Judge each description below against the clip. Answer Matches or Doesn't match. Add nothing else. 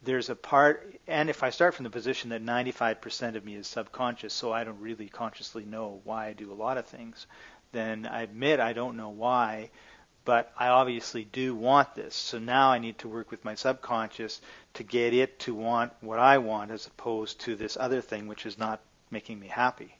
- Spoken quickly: Matches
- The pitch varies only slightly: Matches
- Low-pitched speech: Matches